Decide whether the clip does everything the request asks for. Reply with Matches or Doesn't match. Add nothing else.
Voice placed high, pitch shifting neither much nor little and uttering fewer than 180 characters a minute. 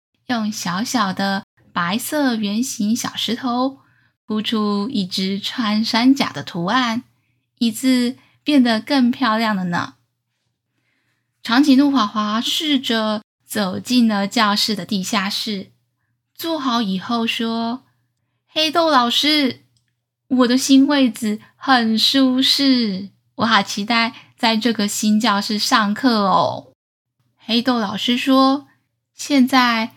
Matches